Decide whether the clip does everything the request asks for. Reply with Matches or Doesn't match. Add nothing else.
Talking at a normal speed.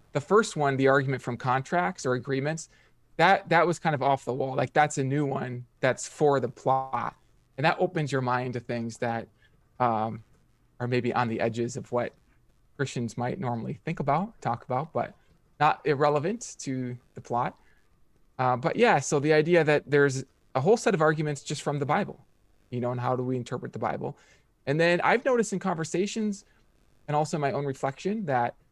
Matches